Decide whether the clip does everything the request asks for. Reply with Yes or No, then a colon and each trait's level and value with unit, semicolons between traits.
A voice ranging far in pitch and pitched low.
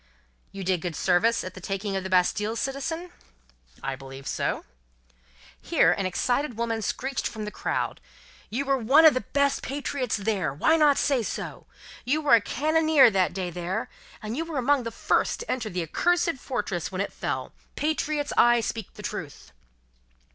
No: wide, 6.9 semitones; high, 230 Hz